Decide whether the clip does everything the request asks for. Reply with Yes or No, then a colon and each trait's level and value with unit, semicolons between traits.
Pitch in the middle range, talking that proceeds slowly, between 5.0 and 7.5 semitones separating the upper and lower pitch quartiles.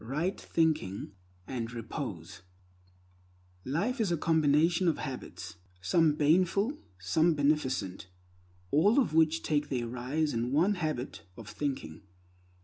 Yes: medium, 150 Hz; slow, 125 wpm; average, 5.3 semitones